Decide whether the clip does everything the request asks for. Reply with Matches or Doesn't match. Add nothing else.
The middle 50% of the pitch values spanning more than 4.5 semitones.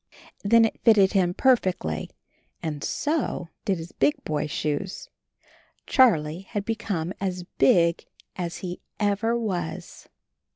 Matches